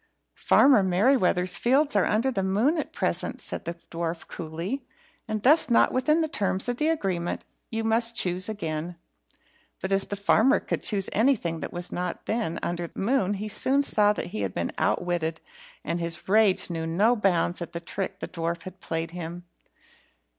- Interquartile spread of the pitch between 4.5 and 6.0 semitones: Yes, average, 4.9 semitones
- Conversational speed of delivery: Yes, average, 180 wpm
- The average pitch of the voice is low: No, high, 190 Hz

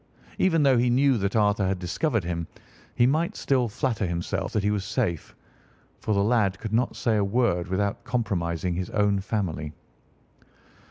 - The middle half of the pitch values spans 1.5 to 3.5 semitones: No, average, 4.5 semitones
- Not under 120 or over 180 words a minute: Yes, average, 170 wpm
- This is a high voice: No, low, 105 Hz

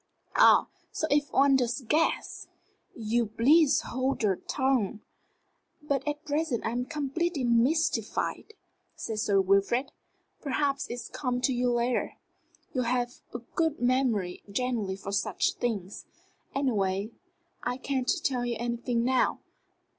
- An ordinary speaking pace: No, slow, 125 wpm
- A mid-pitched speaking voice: No, high, 245 Hz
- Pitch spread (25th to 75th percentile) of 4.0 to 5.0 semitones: No, average, 3.1 semitones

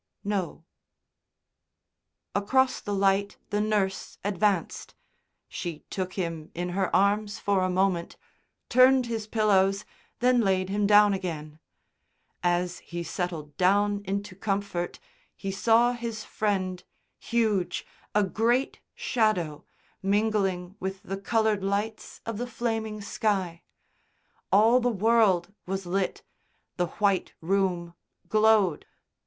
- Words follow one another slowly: Yes, slow, 115 wpm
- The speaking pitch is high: Yes, high, 200 Hz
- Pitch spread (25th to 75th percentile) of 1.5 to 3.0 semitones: Yes, average, 2.7 semitones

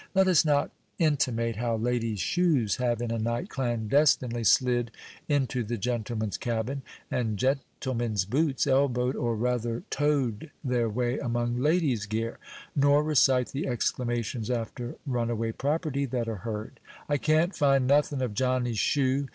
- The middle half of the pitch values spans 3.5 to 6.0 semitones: No, average, 3.1 semitones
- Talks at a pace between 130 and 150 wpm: Yes, average, 145 wpm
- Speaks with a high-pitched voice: No, low, 125 Hz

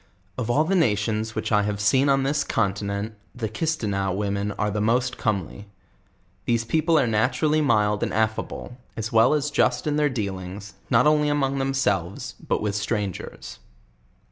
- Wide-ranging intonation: No, average, 4.9 semitones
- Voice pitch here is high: No, low, 110 Hz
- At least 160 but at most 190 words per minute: Yes, average, 170 wpm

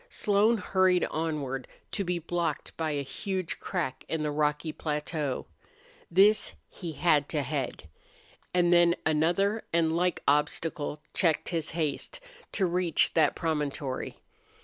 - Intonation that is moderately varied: Yes, average, 3.2 semitones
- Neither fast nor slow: No, slow, 130 wpm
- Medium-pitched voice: Yes, medium, 165 Hz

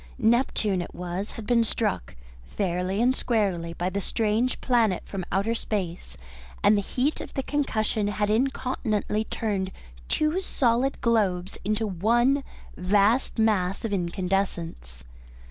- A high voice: Yes, high, 210 Hz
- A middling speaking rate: No, slow, 130 wpm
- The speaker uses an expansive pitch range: No, average, 3.9 semitones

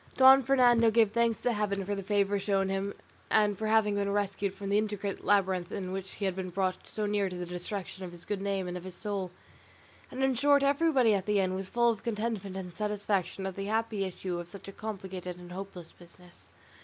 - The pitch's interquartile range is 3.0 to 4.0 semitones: No, narrow, 2.4 semitones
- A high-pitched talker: Yes, high, 200 Hz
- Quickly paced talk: Yes, fast, 225 wpm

